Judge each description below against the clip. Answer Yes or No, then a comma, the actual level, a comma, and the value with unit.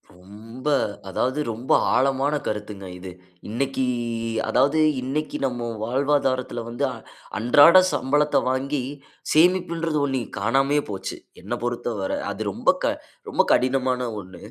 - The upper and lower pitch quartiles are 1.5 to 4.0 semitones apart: Yes, average, 3.7 semitones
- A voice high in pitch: No, low, 130 Hz